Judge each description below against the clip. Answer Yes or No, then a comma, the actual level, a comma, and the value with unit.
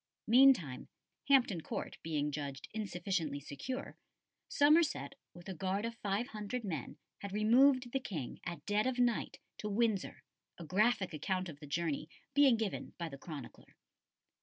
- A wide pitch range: Yes, wide, 6.7 semitones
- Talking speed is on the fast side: No, average, 150 wpm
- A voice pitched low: No, high, 200 Hz